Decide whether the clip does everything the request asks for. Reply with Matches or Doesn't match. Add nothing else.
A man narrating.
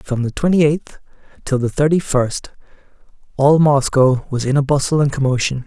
Matches